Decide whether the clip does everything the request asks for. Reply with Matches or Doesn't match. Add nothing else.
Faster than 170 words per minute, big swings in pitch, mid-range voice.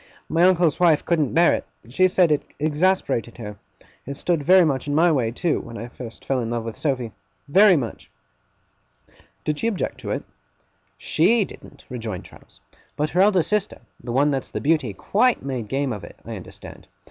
Matches